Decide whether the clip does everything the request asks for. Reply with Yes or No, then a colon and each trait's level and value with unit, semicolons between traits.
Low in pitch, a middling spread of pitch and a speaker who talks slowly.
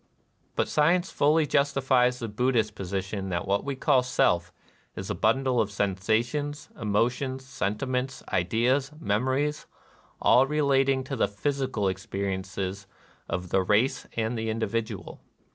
Yes: low, 120 Hz; average, 5.0 semitones; slow, 130 wpm